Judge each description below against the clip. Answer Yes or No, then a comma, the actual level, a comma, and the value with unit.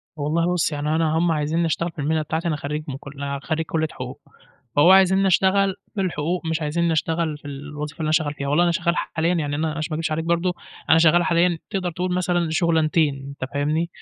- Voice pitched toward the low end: No, medium, 160 Hz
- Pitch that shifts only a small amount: Yes, narrow, 2.3 semitones